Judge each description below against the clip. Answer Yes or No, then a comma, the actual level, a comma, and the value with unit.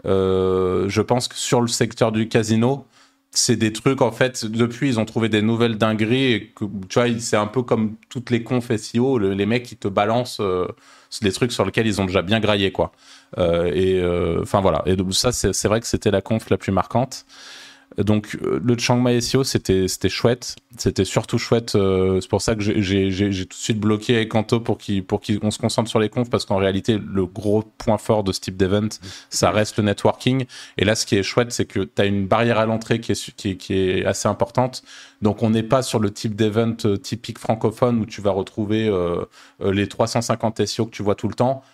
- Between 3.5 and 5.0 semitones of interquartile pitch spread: No, average, 3.0 semitones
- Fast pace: Yes, fast, 225 wpm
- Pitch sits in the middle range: No, low, 110 Hz